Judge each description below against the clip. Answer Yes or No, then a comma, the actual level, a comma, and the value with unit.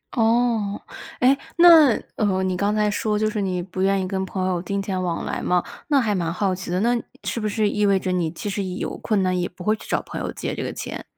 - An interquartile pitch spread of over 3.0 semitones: No, average, 2.7 semitones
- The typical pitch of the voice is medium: No, high, 195 Hz